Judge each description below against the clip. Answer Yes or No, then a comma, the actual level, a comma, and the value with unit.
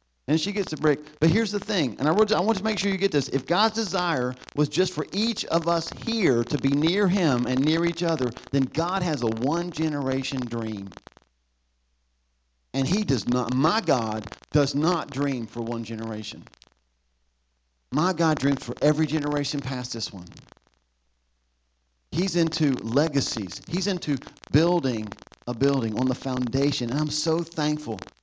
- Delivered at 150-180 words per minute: Yes, average, 170 wpm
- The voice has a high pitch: No, medium, 140 Hz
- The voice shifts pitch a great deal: Yes, wide, 6.6 semitones